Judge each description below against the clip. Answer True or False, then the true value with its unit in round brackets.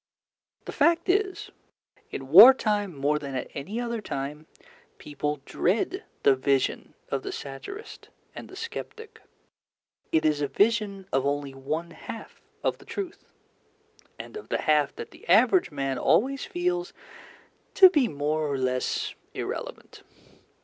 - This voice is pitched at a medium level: True (170 Hz)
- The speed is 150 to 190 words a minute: False (140 wpm)